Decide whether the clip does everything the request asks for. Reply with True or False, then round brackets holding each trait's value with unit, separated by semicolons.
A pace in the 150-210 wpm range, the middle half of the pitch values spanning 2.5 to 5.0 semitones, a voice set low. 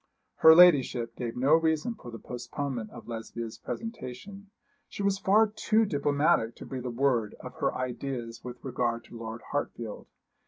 False (160 wpm; 5.5 semitones; 130 Hz)